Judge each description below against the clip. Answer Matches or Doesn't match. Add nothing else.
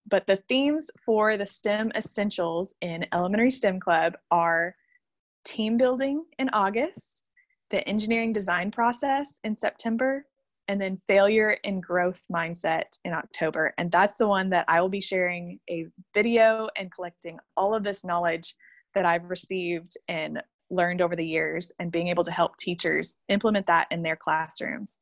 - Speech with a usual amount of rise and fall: Matches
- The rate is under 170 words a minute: Matches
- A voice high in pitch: Matches